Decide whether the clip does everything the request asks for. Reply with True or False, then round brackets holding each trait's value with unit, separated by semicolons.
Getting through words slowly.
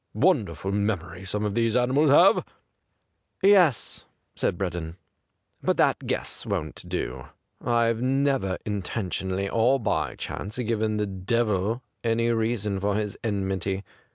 False (155 wpm)